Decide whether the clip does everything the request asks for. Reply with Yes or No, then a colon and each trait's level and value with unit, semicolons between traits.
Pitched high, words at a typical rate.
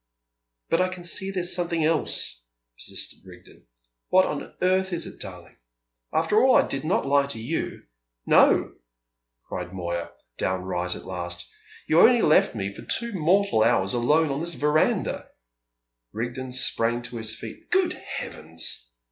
No: medium, 140 Hz; average, 150 wpm